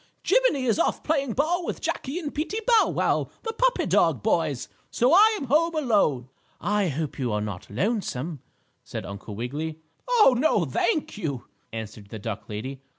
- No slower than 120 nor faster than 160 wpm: No, average, 170 wpm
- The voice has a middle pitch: No, high, 210 Hz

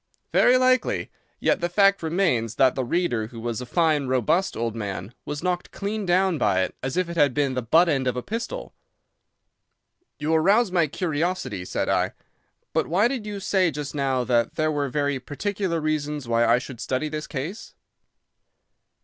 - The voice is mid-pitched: Yes, medium, 150 Hz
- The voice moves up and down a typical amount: No, wide, 6.2 semitones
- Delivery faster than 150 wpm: Yes, average, 185 wpm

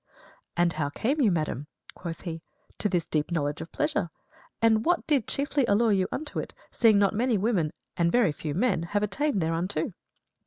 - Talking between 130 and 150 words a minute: No, average, 185 wpm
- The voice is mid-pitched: No, high, 200 Hz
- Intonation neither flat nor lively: No, wide, 6.2 semitones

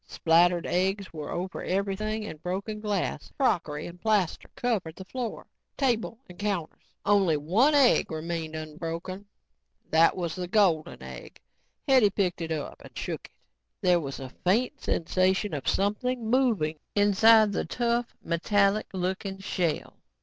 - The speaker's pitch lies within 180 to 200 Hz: Yes, high, 190 Hz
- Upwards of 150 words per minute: No, average, 140 wpm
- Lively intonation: No, average, 4.3 semitones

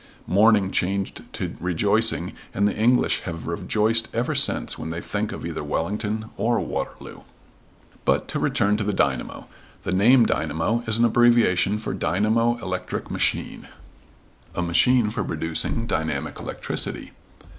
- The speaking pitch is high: No, low, 105 Hz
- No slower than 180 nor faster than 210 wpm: No, average, 140 wpm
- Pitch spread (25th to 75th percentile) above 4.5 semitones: No, average, 4.2 semitones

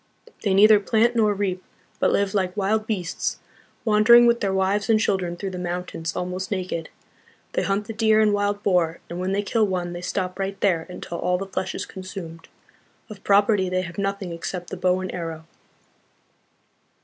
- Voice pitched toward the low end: No, high, 190 Hz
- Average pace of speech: Yes, average, 185 wpm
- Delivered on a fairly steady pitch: Yes, narrow, 2.3 semitones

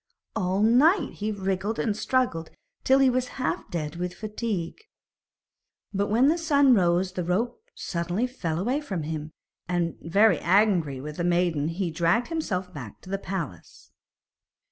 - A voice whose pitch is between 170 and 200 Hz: Yes, high, 190 Hz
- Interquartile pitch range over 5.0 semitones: Yes, wide, 5.5 semitones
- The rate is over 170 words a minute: No, average, 155 wpm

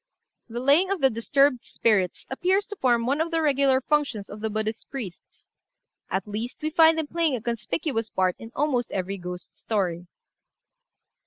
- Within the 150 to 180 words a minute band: Yes, average, 165 wpm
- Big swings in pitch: Yes, wide, 5.8 semitones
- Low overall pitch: No, high, 245 Hz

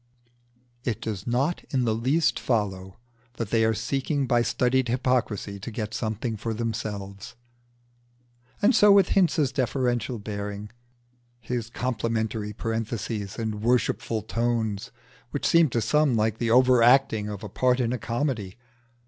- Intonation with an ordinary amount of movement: Yes, average, 3.0 semitones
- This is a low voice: Yes, low, 115 Hz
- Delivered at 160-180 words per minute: No, average, 140 wpm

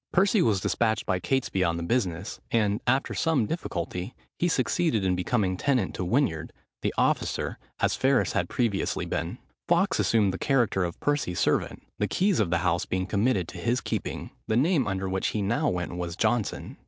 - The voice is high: No, low, 105 Hz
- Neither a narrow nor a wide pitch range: No, wide, 5.9 semitones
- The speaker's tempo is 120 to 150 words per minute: No, average, 185 wpm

